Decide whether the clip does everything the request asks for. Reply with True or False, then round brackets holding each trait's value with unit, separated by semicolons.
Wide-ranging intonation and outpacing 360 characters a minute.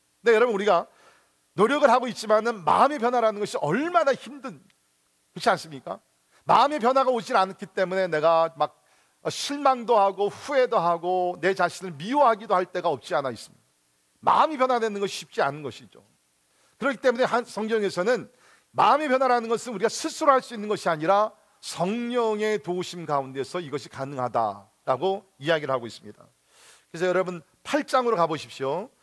True (6.5 semitones; 370 characters per minute)